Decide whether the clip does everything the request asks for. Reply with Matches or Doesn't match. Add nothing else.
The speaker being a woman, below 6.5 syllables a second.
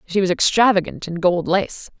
Matches